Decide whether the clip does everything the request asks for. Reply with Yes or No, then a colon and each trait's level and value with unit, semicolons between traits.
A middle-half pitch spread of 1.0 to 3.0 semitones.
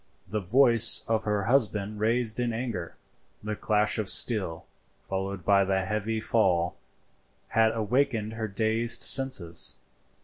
Yes: average, 2.7 semitones